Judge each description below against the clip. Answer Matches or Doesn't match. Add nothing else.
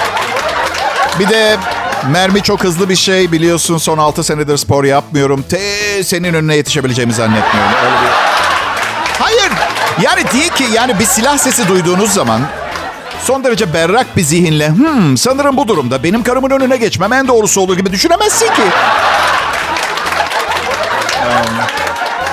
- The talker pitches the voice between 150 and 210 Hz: Matches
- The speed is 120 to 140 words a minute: Matches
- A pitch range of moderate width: Doesn't match